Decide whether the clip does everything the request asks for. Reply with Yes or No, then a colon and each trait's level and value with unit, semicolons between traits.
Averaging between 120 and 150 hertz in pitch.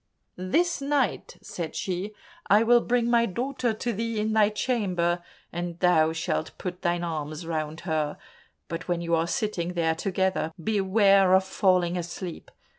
No: medium, 185 Hz